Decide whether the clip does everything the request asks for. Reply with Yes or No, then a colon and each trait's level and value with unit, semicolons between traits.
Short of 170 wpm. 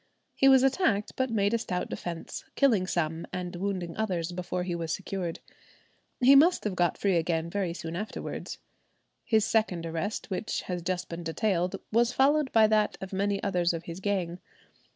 No: average, 175 wpm